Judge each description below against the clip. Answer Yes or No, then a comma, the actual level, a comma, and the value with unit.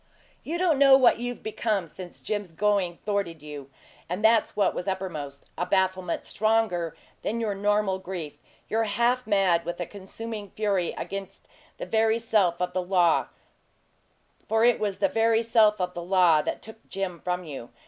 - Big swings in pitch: No, average, 3.8 semitones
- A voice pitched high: Yes, high, 195 Hz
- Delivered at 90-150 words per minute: No, average, 170 wpm